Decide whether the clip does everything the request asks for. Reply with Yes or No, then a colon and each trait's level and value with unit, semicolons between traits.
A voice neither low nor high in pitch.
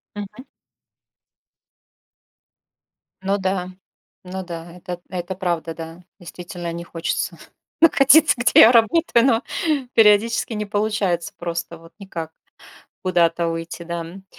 Yes: medium, 180 Hz